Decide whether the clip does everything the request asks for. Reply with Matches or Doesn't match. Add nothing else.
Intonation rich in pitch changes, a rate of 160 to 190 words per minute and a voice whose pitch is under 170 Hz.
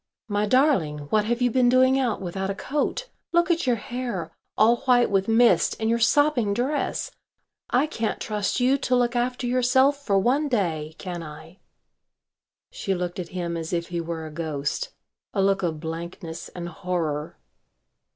Doesn't match